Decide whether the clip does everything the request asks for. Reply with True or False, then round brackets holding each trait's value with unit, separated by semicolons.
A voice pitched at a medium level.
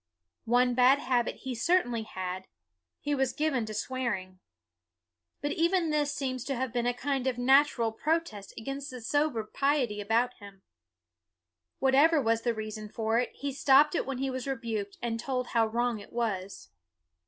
False (245 Hz)